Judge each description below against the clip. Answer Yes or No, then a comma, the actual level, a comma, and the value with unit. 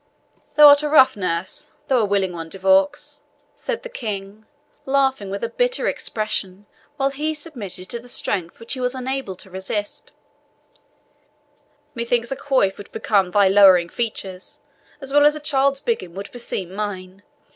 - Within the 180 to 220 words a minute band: No, average, 165 wpm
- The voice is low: No, high, 220 Hz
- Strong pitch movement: Yes, wide, 6.1 semitones